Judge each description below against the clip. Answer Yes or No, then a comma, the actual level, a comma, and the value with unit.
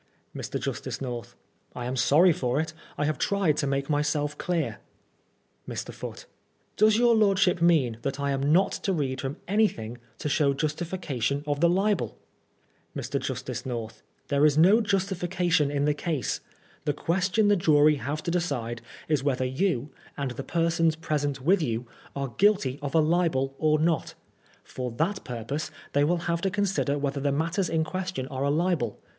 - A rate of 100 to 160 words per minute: No, average, 175 wpm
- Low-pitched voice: No, medium, 150 Hz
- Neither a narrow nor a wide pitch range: Yes, average, 4.4 semitones